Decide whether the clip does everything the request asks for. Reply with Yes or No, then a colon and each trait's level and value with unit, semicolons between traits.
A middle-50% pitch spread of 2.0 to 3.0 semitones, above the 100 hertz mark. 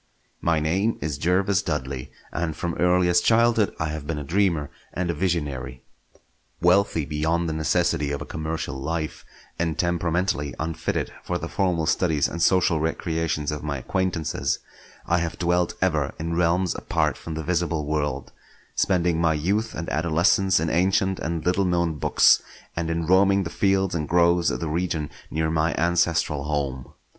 No: narrow, 2.5 semitones; very low, 85 Hz